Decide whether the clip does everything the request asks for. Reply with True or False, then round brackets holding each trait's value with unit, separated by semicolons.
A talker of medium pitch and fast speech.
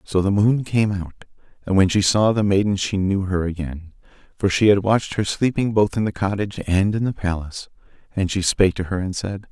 False (100 Hz; 225 wpm)